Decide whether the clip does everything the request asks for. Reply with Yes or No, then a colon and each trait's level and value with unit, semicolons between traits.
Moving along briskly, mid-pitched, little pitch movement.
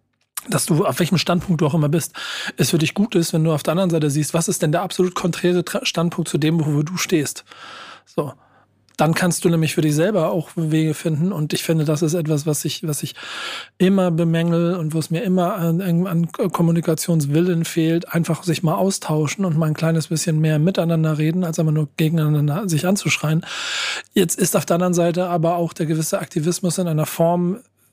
Yes: fast, 210 wpm; medium, 170 Hz; narrow, 1.9 semitones